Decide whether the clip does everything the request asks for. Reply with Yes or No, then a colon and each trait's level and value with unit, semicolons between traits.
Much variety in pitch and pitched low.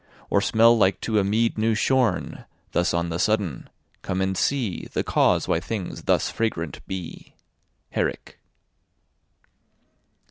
No: average, 4.0 semitones; low, 100 Hz